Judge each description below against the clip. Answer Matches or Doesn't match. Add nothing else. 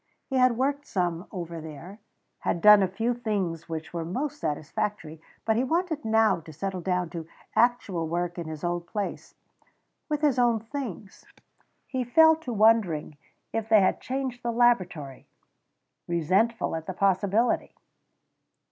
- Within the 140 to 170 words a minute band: Matches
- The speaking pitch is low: Doesn't match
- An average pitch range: Doesn't match